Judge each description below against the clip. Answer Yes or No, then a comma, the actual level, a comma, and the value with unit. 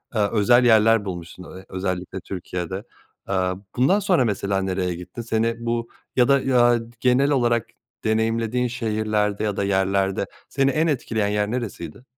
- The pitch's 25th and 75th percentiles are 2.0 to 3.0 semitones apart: No, average, 3.9 semitones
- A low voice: Yes, low, 110 Hz